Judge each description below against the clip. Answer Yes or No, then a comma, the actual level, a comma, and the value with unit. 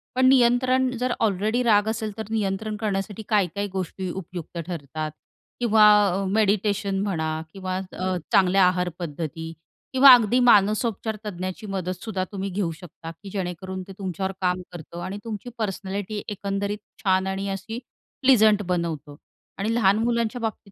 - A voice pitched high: Yes, high, 195 Hz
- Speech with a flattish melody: No, average, 3.0 semitones